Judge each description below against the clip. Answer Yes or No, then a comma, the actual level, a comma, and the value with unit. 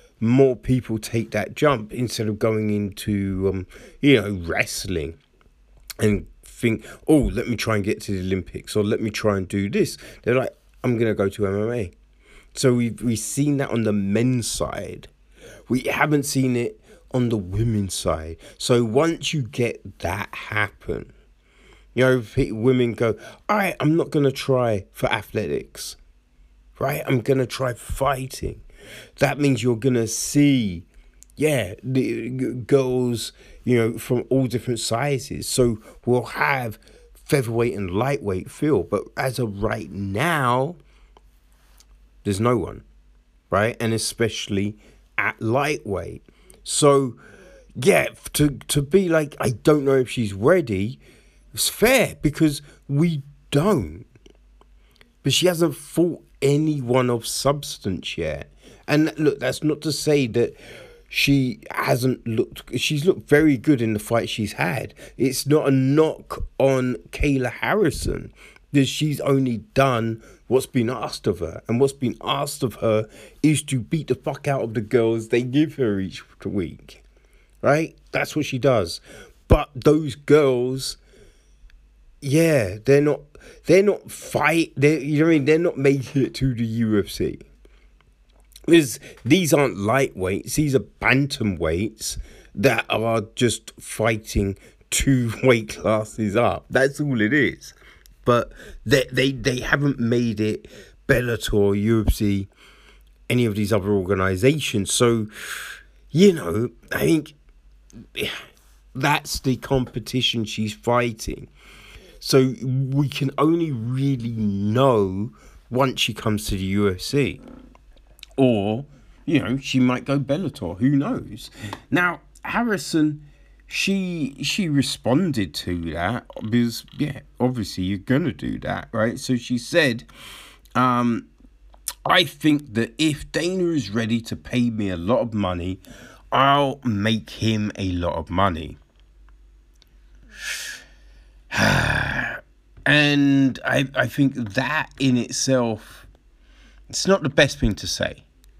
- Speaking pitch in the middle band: No, low, 120 Hz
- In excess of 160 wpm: No, average, 140 wpm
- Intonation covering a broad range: No, average, 4.7 semitones